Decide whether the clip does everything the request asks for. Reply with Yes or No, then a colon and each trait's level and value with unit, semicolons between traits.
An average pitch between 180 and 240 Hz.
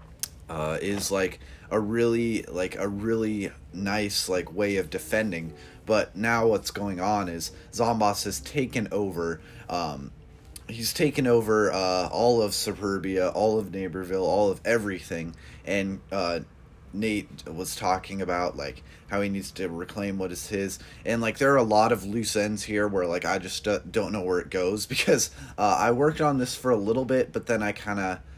No: low, 100 Hz